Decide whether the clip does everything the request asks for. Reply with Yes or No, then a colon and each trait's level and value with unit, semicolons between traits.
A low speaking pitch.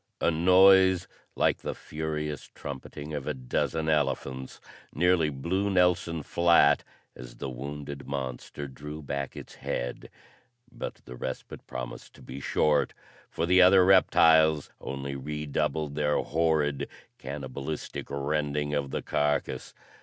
Yes: very low, 75 Hz